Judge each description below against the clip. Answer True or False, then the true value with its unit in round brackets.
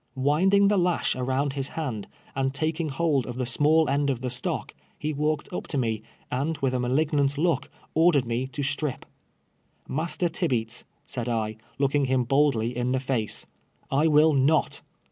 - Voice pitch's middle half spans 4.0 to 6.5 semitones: False (3.5 semitones)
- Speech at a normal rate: True (175 wpm)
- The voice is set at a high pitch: False (140 Hz)